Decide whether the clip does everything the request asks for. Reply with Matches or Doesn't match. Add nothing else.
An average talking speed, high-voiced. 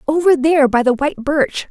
Doesn't match